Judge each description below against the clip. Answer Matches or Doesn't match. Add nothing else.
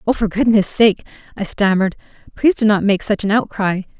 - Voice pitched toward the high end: Matches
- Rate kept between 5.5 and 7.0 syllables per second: Matches